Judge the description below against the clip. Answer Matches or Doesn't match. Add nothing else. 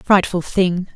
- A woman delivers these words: Matches